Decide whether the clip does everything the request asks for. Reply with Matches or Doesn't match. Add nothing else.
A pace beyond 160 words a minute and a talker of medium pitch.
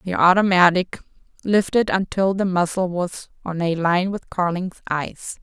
Doesn't match